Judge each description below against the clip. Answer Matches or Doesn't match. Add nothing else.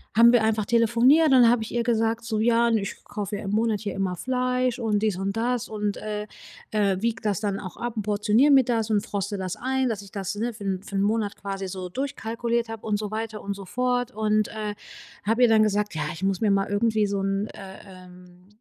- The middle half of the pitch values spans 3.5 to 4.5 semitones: Doesn't match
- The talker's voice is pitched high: Matches